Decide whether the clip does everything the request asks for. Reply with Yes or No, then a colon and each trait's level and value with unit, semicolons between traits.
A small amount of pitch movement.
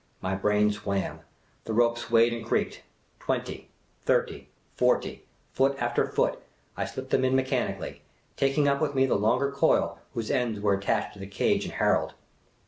No: average, 4.1 semitones